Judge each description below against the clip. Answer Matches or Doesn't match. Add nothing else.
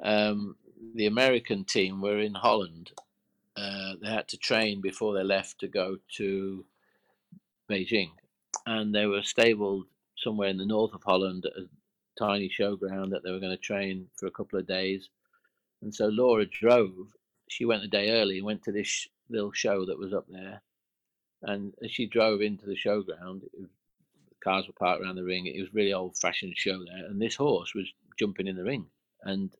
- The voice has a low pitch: Matches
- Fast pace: Doesn't match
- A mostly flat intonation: Matches